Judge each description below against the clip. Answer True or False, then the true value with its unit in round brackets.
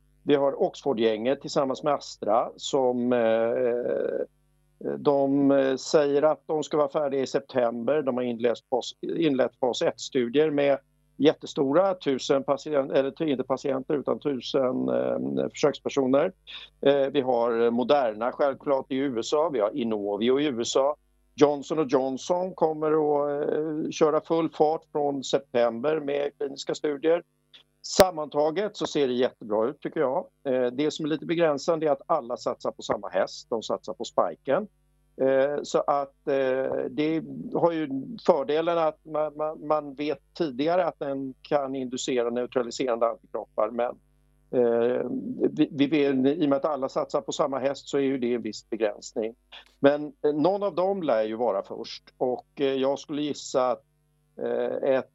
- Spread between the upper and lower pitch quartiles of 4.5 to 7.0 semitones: False (2.9 semitones)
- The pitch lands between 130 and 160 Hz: True (140 Hz)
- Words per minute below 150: True (135 wpm)